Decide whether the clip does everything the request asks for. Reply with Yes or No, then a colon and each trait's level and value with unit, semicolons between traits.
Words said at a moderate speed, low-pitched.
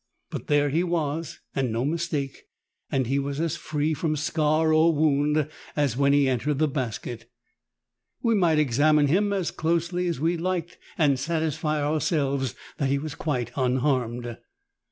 No: average, 155 wpm; medium, 150 Hz